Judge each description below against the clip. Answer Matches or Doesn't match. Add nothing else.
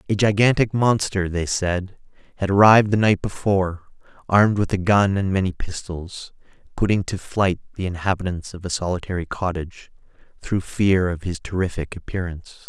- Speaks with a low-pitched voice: Matches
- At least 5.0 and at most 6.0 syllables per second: Matches